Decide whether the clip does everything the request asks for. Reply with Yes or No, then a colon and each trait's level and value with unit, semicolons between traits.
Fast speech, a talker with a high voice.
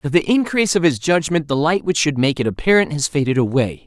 No: fast, 250 wpm; medium, 155 Hz